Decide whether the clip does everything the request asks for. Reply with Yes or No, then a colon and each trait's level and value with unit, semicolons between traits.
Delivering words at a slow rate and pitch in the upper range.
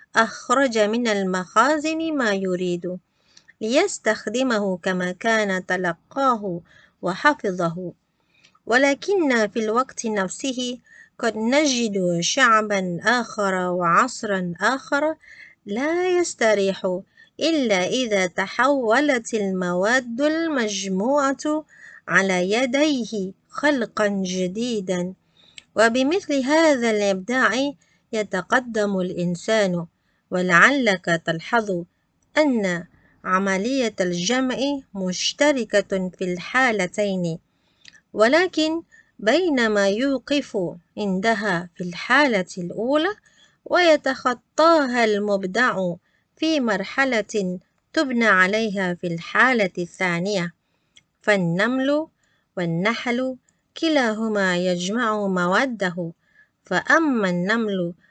Yes: slow, 70 wpm; high, 215 Hz